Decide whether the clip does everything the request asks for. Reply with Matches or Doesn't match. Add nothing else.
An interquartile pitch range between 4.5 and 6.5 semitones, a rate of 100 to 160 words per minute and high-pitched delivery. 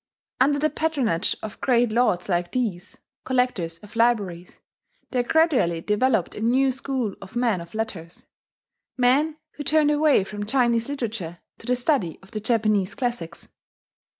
Matches